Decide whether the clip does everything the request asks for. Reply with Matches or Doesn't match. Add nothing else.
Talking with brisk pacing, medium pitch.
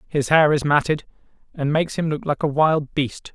Matches